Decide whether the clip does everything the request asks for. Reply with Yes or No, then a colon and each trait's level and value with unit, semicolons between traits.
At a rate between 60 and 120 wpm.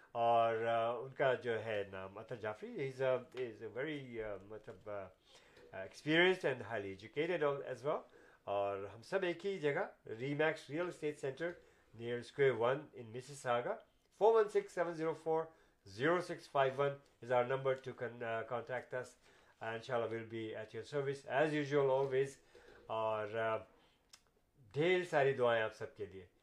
No: average, 150 wpm